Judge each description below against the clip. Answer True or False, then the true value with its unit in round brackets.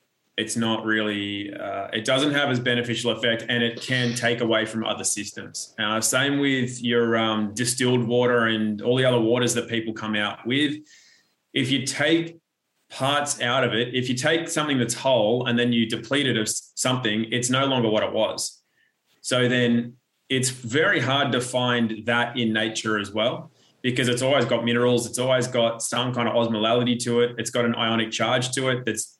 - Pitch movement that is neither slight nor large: False (2.1 semitones)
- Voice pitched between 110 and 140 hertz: True (120 Hz)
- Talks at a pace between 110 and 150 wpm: False (195 wpm)